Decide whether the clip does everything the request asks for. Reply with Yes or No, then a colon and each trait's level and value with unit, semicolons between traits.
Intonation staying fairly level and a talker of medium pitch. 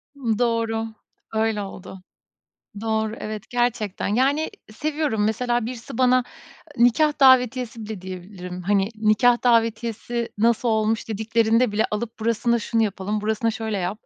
No: narrow, 2.1 semitones; high, 225 Hz